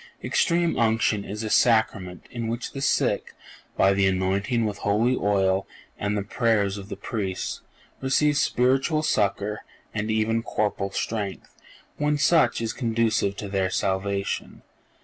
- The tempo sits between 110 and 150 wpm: Yes, average, 140 wpm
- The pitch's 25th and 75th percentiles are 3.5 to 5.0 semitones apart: No, average, 3.1 semitones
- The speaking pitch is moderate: No, low, 110 Hz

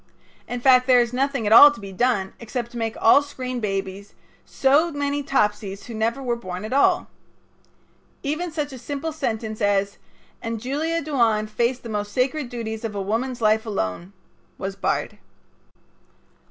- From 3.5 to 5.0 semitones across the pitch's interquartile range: Yes, average, 4.3 semitones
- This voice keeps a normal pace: Yes, average, 165 wpm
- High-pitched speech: Yes, high, 235 Hz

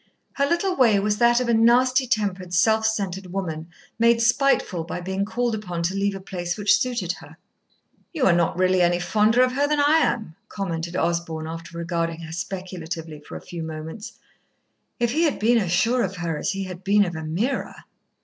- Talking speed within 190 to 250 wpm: Yes, average, 195 wpm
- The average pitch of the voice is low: No, high, 195 Hz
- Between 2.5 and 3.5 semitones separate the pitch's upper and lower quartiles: No, average, 5.3 semitones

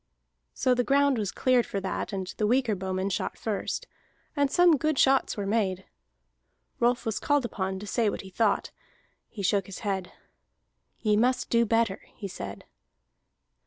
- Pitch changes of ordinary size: Yes, average, 4.4 semitones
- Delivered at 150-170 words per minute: Yes, average, 165 wpm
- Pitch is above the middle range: Yes, high, 220 Hz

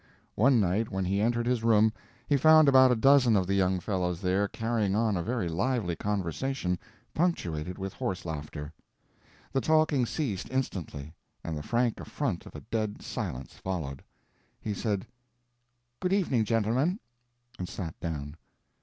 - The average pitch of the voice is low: Yes, low, 105 Hz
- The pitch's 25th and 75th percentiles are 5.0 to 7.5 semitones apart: Yes, wide, 5.6 semitones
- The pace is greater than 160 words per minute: No, average, 155 wpm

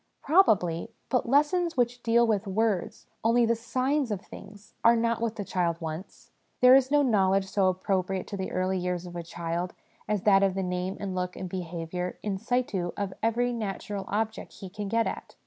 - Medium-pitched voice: No, high, 200 Hz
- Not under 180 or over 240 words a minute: Yes, average, 195 wpm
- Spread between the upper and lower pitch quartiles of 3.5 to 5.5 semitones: Yes, average, 4.1 semitones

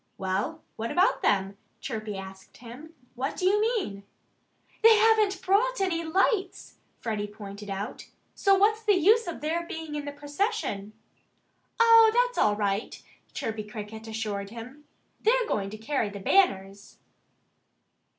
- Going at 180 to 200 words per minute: No, average, 140 wpm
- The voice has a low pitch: No, very high, 285 Hz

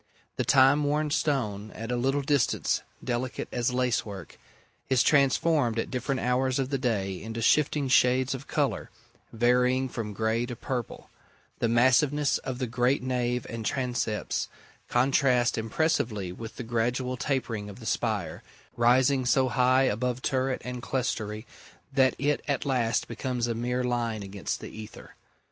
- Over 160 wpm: No, average, 150 wpm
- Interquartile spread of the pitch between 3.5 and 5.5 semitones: No, narrow, 2.4 semitones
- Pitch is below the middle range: Yes, low, 125 Hz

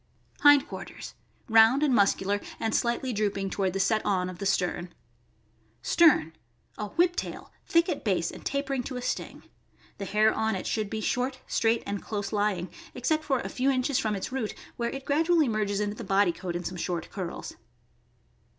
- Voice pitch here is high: Yes, high, 215 Hz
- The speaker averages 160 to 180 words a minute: No, average, 200 wpm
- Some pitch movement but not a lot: Yes, average, 5.0 semitones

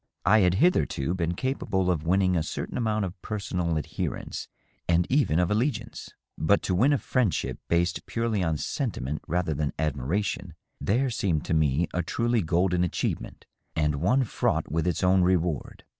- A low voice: Yes, very low, 90 Hz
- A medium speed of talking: Yes, average, 170 wpm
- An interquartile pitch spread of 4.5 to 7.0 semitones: Yes, average, 4.8 semitones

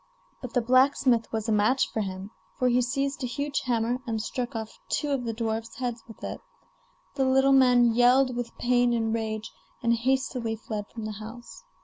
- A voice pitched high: Yes, high, 240 Hz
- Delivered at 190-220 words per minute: Yes, average, 195 wpm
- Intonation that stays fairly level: Yes, narrow, 2.3 semitones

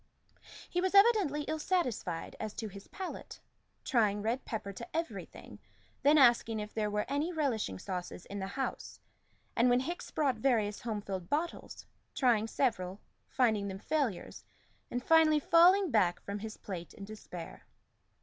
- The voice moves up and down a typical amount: No, wide, 6.7 semitones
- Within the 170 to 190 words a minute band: No, average, 155 wpm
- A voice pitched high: Yes, high, 230 Hz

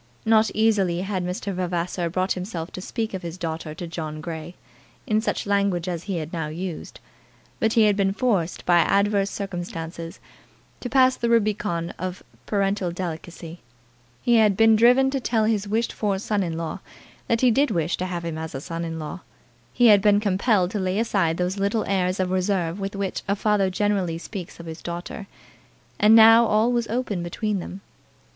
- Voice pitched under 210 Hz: Yes, high, 190 Hz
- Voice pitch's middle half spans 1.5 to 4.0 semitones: Yes, average, 3.7 semitones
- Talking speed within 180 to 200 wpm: Yes, average, 190 wpm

